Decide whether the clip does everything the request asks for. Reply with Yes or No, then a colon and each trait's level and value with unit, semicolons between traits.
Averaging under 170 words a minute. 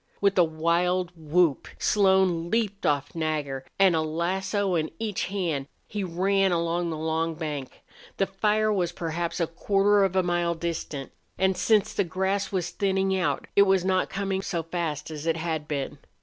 No: average, 175 wpm